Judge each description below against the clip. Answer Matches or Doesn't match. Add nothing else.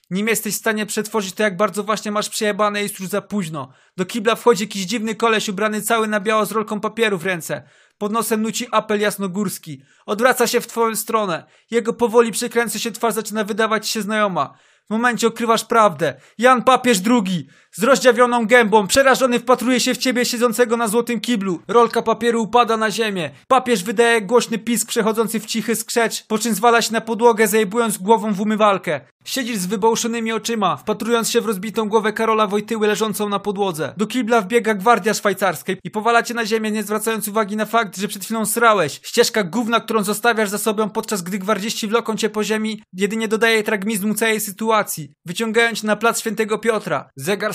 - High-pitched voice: Matches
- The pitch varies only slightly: Matches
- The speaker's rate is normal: Doesn't match